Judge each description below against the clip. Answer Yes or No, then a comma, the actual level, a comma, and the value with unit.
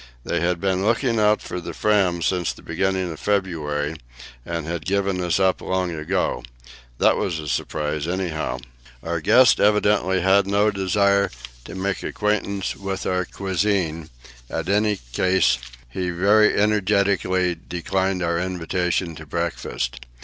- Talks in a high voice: No, very low, 95 Hz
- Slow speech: No, average, 145 wpm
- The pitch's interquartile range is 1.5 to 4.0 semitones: Yes, average, 2.8 semitones